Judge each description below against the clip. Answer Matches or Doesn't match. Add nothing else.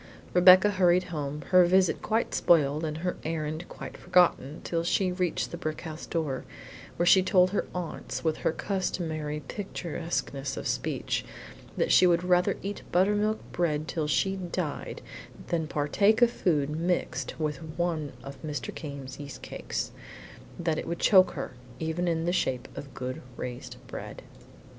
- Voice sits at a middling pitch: Matches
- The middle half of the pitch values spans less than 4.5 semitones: Matches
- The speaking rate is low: Doesn't match